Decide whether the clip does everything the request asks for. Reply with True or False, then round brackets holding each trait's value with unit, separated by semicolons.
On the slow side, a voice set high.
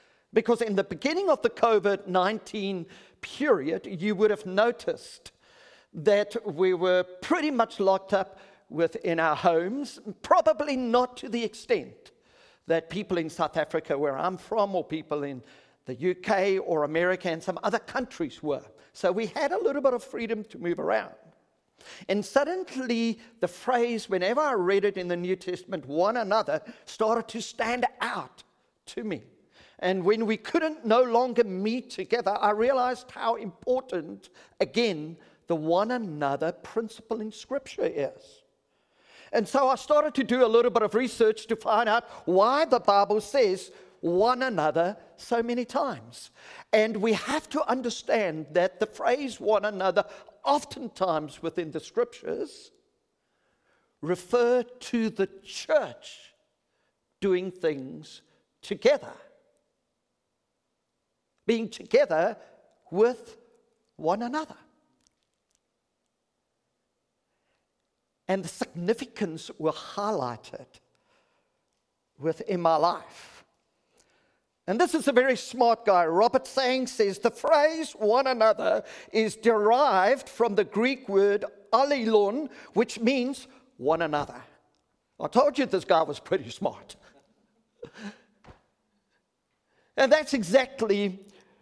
True (125 wpm; 220 Hz)